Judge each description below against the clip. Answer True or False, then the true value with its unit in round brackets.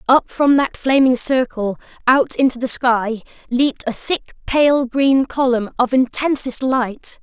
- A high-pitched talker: True (255 Hz)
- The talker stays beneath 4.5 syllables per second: True (4.2 syllables/s)